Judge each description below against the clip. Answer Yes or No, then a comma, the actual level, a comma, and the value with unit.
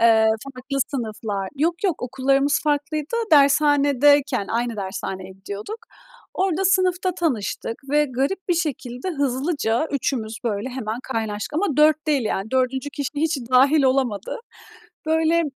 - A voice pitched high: Yes, very high, 275 Hz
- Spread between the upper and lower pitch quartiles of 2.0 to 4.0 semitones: No, average, 4.8 semitones